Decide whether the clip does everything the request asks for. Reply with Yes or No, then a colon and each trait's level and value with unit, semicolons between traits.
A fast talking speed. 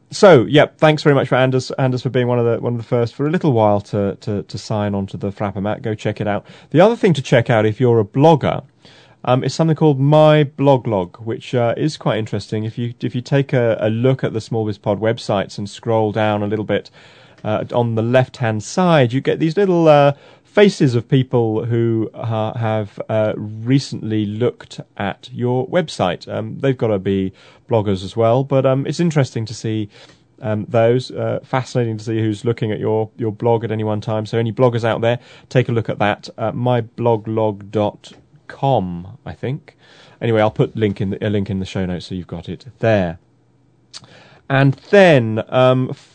Yes: fast, 210 wpm